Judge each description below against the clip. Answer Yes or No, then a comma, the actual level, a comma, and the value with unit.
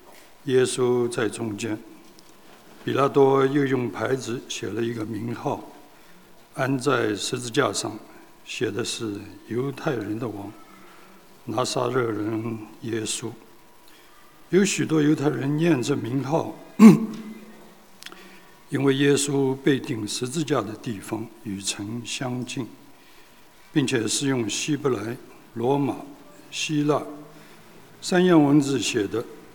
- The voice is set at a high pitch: No, low, 135 Hz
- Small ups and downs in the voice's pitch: No, average, 4.7 semitones